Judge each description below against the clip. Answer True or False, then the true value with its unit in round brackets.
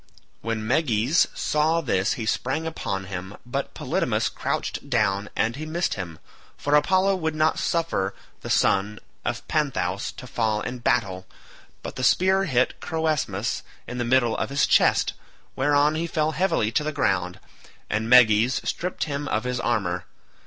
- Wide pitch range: True (6.7 semitones)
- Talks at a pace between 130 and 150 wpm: False (160 wpm)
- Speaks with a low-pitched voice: True (125 Hz)